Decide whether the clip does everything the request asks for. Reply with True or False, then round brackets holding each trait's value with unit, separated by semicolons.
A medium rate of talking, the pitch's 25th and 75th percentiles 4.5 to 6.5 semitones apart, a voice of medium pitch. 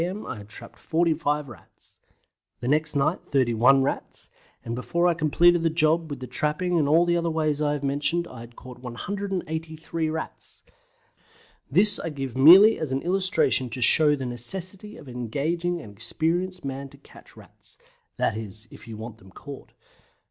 True (170 wpm; 4.9 semitones; 150 Hz)